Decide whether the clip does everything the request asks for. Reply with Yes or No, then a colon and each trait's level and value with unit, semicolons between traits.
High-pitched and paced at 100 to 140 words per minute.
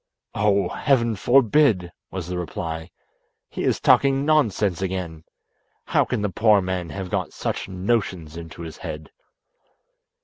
No: very low, 95 Hz; slow, 135 wpm